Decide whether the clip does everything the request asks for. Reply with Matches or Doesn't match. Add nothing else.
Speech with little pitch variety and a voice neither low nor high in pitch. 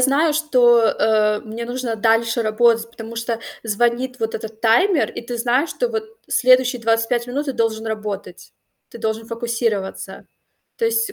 Doesn't match